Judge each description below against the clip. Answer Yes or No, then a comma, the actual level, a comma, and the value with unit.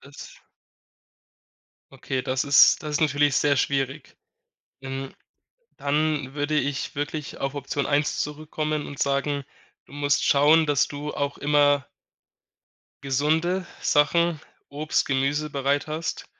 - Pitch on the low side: No, medium, 145 Hz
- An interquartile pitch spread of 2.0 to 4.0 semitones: No, narrow, 1.5 semitones